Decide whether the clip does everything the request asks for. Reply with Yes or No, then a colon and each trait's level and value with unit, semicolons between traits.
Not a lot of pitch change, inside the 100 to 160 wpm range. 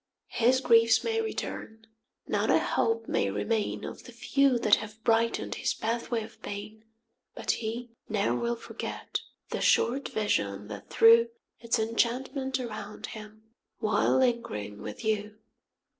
Yes: narrow, 2.0 semitones; average, 145 wpm